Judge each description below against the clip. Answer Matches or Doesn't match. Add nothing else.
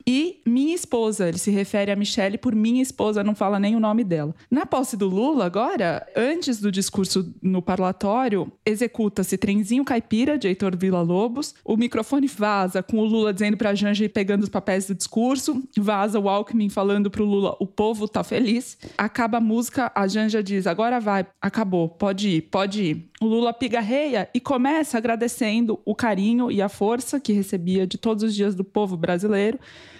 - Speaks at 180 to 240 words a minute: Matches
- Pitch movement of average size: Matches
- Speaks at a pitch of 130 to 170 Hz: Doesn't match